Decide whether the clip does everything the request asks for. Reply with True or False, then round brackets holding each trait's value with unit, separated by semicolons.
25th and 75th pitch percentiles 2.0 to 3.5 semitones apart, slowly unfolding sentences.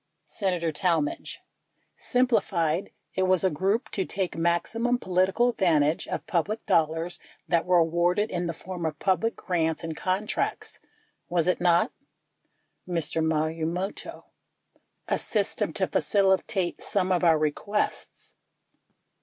True (2.8 semitones; 125 wpm)